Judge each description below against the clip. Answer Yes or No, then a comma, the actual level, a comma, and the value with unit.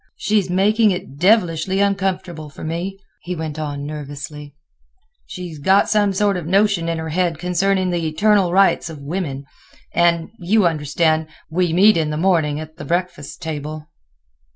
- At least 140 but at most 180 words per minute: Yes, average, 150 wpm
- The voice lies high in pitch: No, medium, 170 Hz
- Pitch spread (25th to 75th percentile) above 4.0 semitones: No, average, 3.6 semitones